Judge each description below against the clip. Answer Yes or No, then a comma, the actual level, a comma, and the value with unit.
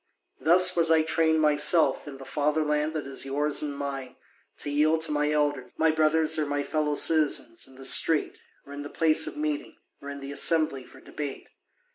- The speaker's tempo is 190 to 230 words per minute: Yes, average, 195 wpm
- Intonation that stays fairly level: Yes, narrow, 1.8 semitones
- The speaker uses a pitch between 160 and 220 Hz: No, medium, 150 Hz